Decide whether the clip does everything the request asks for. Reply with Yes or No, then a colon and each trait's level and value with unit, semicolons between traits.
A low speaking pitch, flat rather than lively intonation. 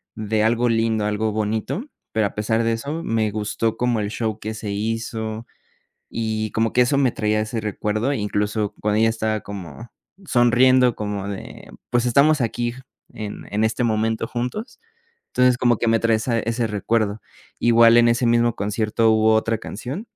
Yes: low, 110 Hz; narrow, 1.7 semitones